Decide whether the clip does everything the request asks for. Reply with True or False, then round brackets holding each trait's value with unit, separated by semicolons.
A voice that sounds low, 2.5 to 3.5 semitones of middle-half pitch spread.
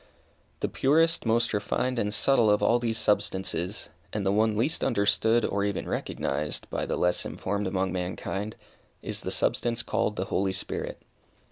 True (105 Hz; 3.2 semitones)